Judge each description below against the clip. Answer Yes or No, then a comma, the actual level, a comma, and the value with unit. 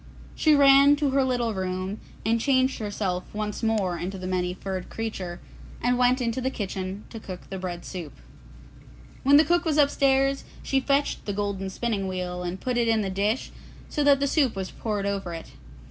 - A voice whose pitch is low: No, high, 215 Hz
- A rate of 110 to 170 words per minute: No, average, 190 wpm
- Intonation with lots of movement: Yes, wide, 6.0 semitones